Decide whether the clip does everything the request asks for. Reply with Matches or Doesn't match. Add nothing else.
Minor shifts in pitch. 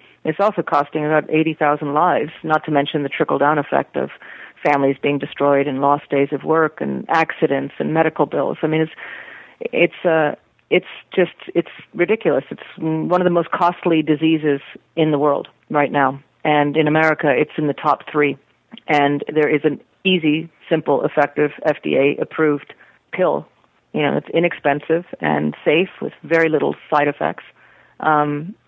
Matches